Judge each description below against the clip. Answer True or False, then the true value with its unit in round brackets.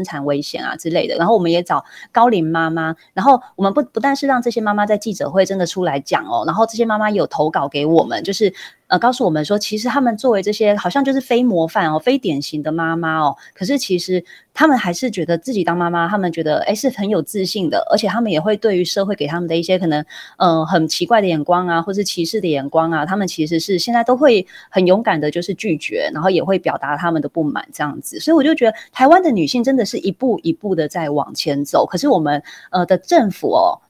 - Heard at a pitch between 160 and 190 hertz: True (185 Hz)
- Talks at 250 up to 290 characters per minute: False (370 characters per minute)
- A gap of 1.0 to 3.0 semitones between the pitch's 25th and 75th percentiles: False (5.5 semitones)